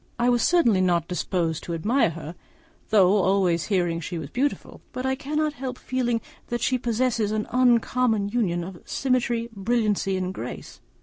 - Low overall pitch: No, high, 220 Hz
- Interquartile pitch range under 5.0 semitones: No, wide, 5.4 semitones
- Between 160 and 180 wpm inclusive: Yes, average, 165 wpm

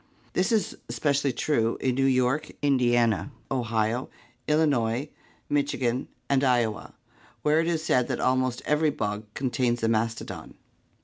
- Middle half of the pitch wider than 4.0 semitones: No, average, 3.7 semitones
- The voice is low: Yes, low, 130 Hz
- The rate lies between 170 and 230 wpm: No, slow, 135 wpm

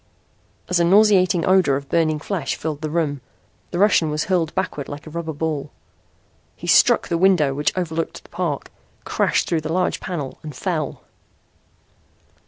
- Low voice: No, medium, 160 Hz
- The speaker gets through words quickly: No, average, 165 wpm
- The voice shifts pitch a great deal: No, average, 3.2 semitones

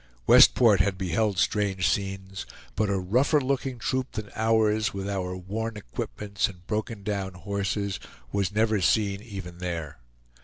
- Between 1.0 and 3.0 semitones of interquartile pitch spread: Yes, narrow, 2.5 semitones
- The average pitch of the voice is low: Yes, low, 100 Hz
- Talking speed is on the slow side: No, average, 145 wpm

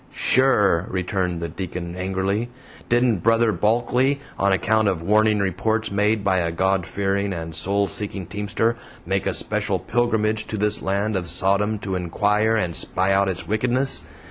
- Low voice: Yes, low, 100 Hz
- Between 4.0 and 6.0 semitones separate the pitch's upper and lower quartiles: No, average, 2.7 semitones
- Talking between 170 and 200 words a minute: No, average, 160 wpm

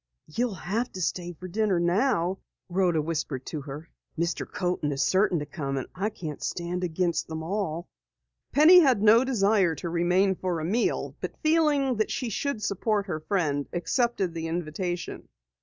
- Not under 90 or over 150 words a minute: No, average, 170 wpm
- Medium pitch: Yes, medium, 180 Hz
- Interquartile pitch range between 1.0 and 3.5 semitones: No, average, 4.5 semitones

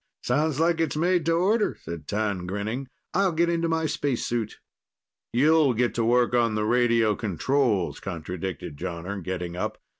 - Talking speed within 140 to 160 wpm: Yes, average, 155 wpm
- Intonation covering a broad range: Yes, wide, 8.3 semitones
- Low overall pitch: Yes, low, 120 Hz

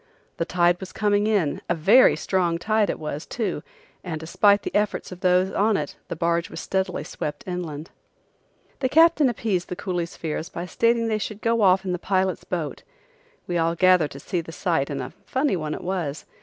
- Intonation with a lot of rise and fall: No, average, 3.7 semitones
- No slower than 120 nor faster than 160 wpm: No, fast, 205 wpm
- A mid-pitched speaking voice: Yes, medium, 180 Hz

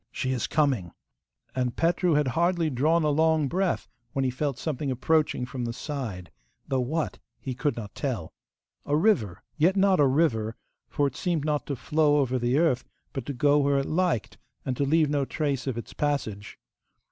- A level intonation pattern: No, average, 3.8 semitones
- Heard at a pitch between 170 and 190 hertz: No, medium, 140 Hz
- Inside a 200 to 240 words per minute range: No, average, 190 wpm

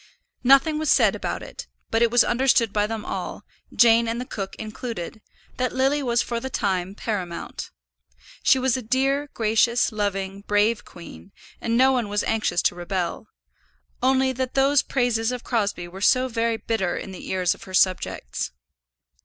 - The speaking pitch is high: Yes, high, 230 Hz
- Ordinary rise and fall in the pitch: Yes, average, 4.1 semitones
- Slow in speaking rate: No, average, 170 wpm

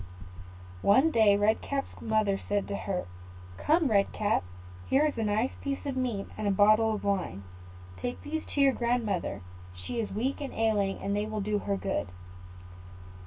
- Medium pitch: No, high, 215 Hz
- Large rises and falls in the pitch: No, average, 4.1 semitones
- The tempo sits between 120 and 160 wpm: No, average, 175 wpm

